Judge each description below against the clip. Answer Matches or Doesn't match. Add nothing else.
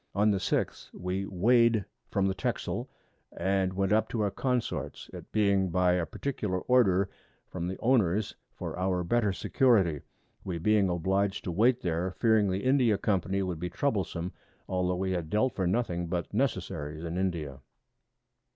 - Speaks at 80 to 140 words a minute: Doesn't match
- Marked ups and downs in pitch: Doesn't match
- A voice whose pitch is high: Doesn't match